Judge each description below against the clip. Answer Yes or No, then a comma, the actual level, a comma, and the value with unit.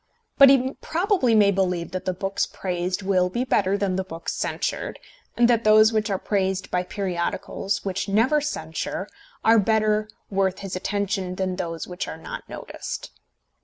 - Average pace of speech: Yes, average, 165 wpm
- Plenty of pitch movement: No, average, 2.9 semitones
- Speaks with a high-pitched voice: Yes, high, 195 Hz